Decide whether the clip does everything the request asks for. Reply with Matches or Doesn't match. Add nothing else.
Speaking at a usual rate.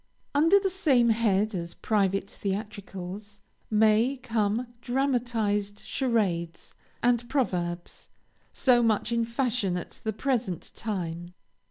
Doesn't match